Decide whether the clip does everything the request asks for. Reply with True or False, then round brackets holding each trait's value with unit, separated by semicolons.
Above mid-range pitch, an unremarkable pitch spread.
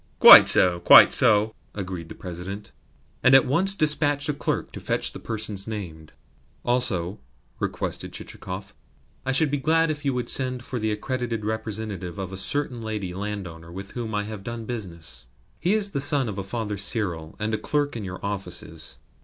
False (110 Hz; 5.0 semitones)